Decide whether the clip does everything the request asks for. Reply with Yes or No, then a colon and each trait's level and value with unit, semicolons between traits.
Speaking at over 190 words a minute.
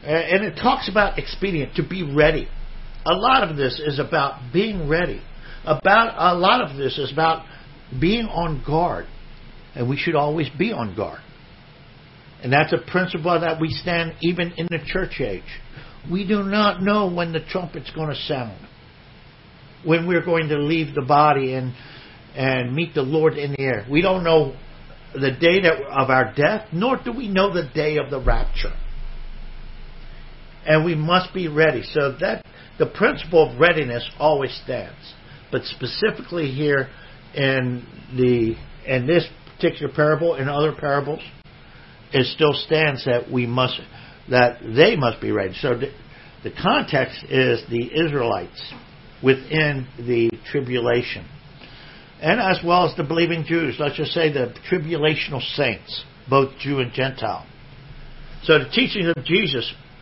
No: average, 155 wpm